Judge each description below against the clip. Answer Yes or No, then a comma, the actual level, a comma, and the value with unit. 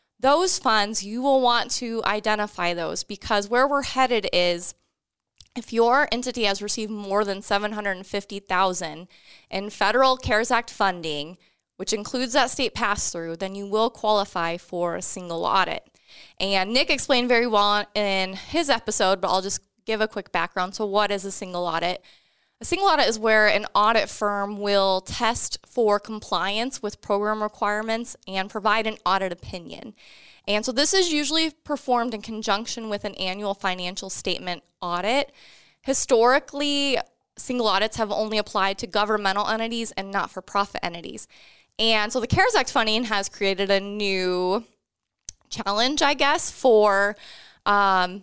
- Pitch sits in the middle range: No, high, 210 Hz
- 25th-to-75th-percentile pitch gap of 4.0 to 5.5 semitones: No, average, 3.5 semitones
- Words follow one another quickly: No, average, 160 wpm